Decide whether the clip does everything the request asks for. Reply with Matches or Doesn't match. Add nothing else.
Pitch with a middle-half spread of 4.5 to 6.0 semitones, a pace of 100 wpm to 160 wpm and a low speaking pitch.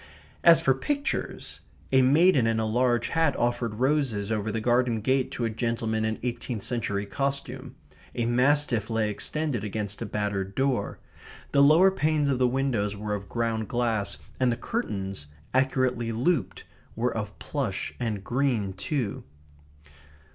Doesn't match